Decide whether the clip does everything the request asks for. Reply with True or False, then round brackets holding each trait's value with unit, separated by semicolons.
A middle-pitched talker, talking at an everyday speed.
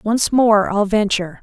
False (210 Hz; 170 wpm)